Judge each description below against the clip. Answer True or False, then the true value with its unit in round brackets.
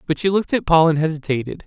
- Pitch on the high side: False (165 Hz)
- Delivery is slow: False (255 wpm)